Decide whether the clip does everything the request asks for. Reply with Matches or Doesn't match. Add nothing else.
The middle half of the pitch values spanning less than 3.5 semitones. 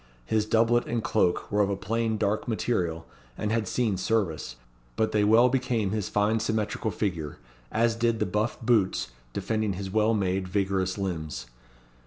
Matches